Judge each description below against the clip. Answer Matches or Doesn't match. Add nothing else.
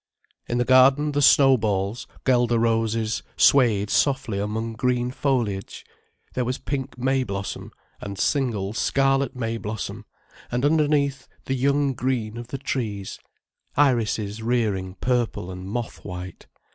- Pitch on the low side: Matches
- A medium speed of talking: Doesn't match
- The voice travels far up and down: Doesn't match